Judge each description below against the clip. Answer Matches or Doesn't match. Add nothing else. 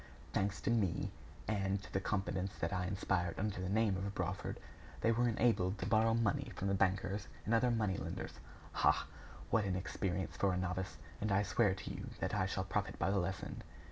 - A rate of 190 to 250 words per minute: Matches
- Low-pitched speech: Matches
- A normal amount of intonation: Doesn't match